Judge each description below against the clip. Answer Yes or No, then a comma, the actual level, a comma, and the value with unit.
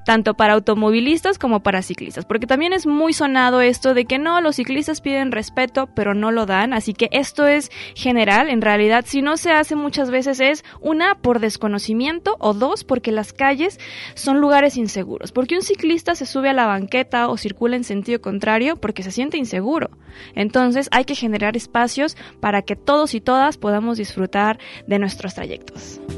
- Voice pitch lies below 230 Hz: No, high, 245 Hz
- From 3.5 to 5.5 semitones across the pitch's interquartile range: Yes, average, 4.9 semitones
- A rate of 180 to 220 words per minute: Yes, average, 185 wpm